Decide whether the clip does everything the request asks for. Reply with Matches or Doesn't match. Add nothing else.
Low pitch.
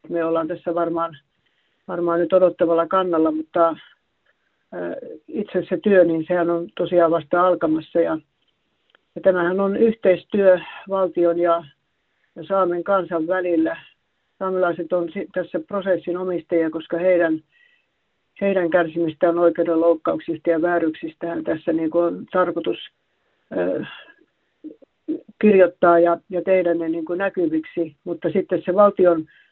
Doesn't match